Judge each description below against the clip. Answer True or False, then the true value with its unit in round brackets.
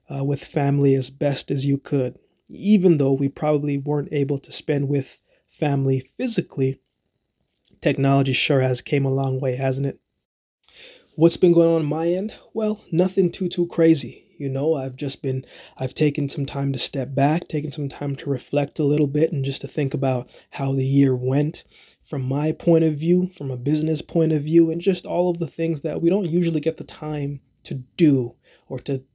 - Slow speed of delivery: False (200 wpm)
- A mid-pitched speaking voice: True (145 Hz)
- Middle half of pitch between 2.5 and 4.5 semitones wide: True (3.0 semitones)